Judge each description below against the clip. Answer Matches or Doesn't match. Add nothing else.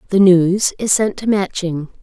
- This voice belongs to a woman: Matches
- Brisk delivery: Doesn't match